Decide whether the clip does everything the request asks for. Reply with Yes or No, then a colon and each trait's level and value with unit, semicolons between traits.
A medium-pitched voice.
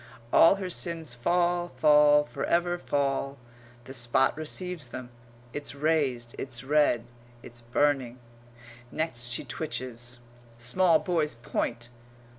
Yes: medium, 145 Hz